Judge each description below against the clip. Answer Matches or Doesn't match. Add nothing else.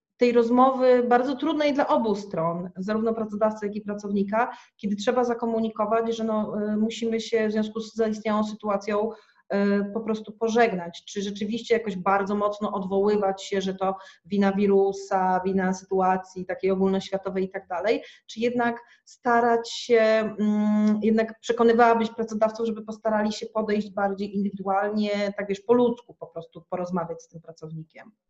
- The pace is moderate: Matches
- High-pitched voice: Matches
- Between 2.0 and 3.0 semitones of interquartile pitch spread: Matches